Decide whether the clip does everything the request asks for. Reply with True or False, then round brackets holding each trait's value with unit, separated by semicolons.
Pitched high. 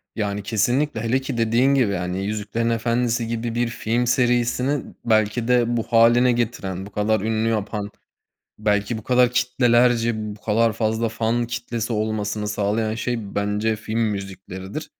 False (115 Hz)